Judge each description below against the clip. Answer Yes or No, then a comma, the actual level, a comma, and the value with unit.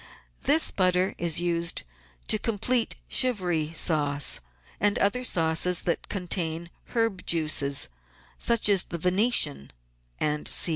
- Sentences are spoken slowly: Yes, slow, 110 wpm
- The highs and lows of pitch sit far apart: No, average, 4.3 semitones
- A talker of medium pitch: Yes, medium, 180 Hz